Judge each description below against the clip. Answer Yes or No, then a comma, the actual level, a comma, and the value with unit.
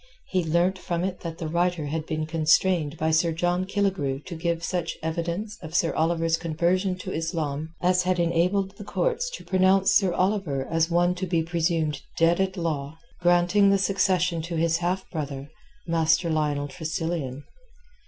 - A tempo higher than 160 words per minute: Yes, average, 170 wpm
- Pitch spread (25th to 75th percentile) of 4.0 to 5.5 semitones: No, narrow, 2.4 semitones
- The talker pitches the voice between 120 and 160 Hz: No, medium, 170 Hz